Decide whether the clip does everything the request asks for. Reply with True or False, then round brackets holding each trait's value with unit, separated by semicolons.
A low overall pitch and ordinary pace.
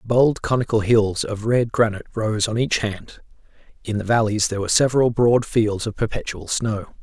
True (110 Hz; 180 wpm)